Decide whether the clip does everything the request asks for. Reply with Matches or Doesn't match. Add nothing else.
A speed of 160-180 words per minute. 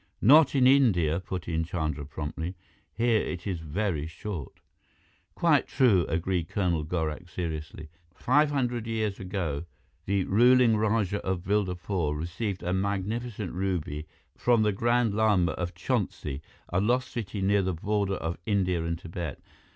Doesn't match